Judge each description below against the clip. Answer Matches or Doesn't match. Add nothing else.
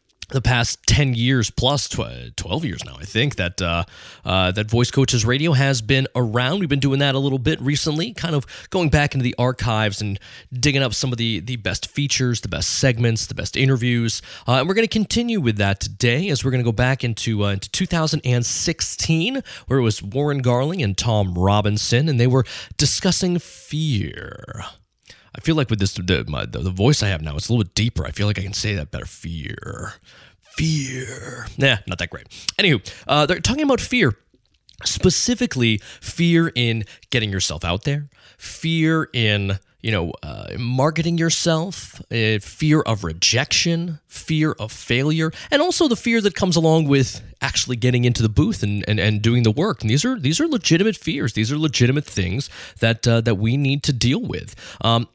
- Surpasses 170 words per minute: Matches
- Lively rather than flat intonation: Matches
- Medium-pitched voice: Doesn't match